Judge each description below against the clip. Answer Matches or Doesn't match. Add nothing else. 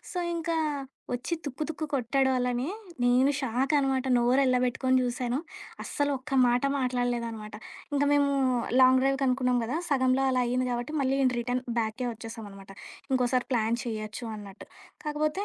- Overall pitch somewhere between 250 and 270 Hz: Matches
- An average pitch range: Doesn't match